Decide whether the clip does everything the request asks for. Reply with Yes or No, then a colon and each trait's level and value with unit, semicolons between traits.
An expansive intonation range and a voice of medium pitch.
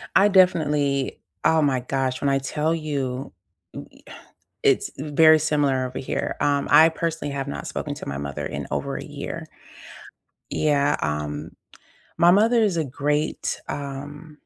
No: average, 2.8 semitones; medium, 145 Hz